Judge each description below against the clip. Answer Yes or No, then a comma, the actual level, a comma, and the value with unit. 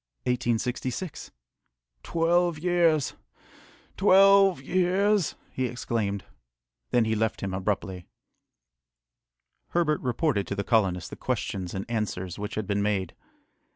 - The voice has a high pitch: No, low, 115 Hz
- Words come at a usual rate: No, slow, 105 wpm